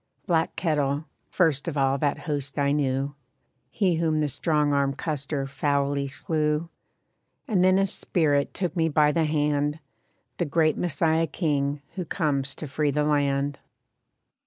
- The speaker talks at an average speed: Yes, average, 150 wpm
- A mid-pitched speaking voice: Yes, medium, 150 Hz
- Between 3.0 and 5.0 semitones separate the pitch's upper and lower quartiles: No, narrow, 2.4 semitones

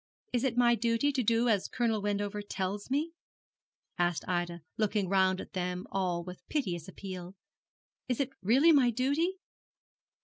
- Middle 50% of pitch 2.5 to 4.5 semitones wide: No, average, 5.0 semitones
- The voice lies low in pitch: No, high, 205 Hz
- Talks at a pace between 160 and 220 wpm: No, average, 150 wpm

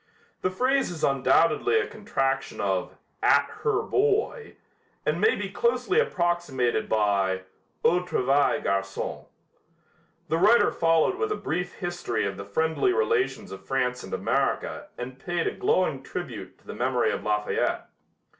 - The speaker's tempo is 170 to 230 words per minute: No, average, 145 wpm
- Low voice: No, medium, 160 Hz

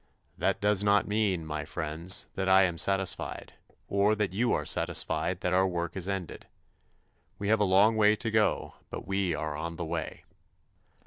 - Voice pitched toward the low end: Yes, very low, 95 Hz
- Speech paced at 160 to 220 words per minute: Yes, average, 180 wpm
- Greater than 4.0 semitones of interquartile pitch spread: No, average, 3.3 semitones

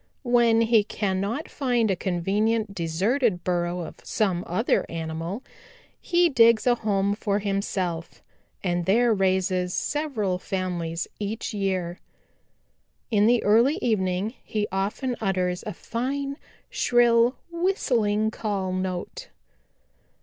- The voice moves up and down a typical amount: Yes, average, 4.1 semitones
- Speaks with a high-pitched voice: Yes, high, 205 Hz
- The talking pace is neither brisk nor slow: No, slow, 115 wpm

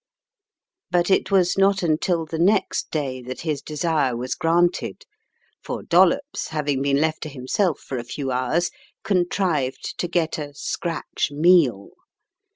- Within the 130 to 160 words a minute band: Yes, average, 150 wpm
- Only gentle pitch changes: No, average, 4.1 semitones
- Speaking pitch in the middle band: Yes, medium, 160 Hz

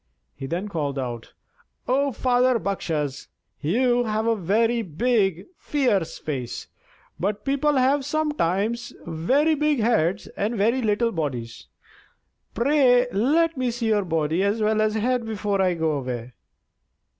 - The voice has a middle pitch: No, high, 215 Hz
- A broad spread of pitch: Yes, wide, 6.9 semitones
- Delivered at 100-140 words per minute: Yes, slow, 135 wpm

